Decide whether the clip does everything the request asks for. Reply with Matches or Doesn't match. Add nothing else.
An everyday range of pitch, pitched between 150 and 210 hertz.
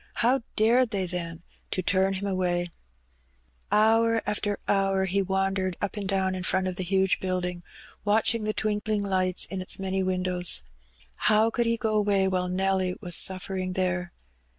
Doesn't match